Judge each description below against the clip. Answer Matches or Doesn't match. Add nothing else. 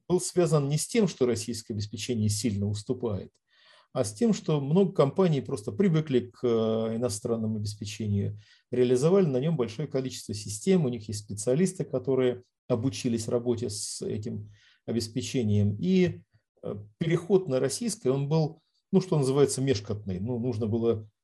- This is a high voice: Doesn't match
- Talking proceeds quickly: Doesn't match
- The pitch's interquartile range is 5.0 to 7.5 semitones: Matches